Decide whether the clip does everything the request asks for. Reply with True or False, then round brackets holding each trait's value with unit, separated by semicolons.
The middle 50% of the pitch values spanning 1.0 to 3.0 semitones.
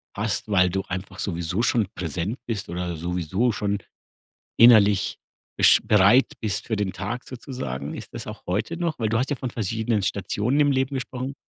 False (4.8 semitones)